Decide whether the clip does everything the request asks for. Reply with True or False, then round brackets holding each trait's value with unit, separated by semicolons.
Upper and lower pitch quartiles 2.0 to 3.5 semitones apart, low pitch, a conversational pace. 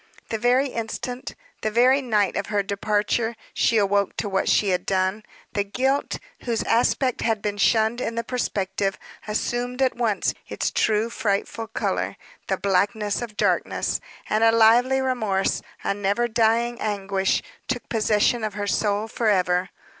False (2.9 semitones; 220 Hz; 155 wpm)